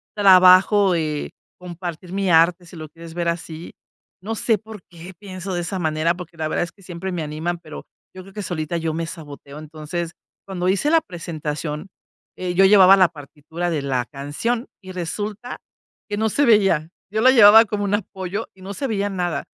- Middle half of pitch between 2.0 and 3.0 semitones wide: No, average, 3.5 semitones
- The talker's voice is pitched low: No, medium, 180 Hz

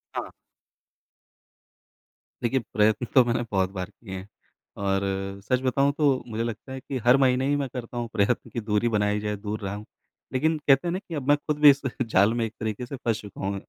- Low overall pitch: Yes, low, 120 Hz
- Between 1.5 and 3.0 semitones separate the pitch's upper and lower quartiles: No, average, 4.2 semitones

